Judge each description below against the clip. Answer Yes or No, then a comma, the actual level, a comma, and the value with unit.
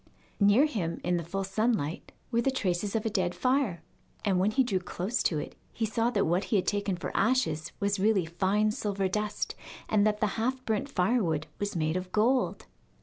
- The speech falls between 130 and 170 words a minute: No, fast, 205 wpm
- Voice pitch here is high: Yes, high, 205 Hz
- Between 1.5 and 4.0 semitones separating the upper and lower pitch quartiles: Yes, average, 3.7 semitones